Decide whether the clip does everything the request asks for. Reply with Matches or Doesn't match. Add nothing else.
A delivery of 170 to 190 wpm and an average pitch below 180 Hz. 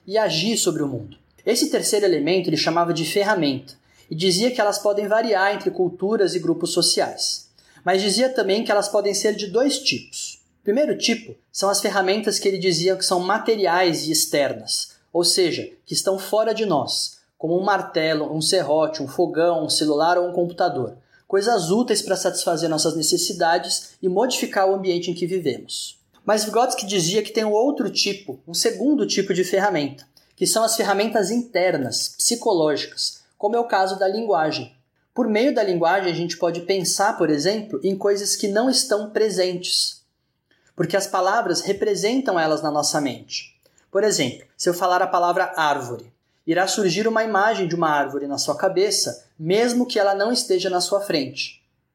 Doesn't match